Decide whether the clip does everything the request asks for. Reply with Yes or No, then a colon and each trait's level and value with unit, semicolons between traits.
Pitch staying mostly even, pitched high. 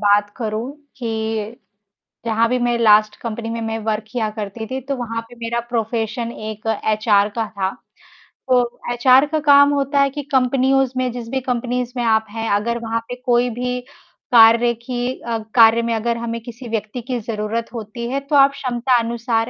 Yes: narrow, 2.0 semitones; high, 235 Hz